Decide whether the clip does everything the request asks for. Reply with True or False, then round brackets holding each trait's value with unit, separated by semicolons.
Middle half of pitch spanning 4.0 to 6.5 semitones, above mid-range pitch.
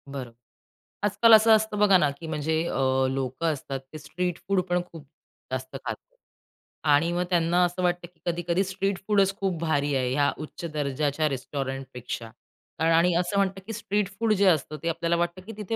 False (4.8 semitones; 170 Hz)